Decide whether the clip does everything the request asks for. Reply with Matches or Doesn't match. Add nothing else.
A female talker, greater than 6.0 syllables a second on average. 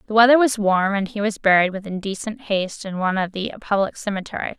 Matches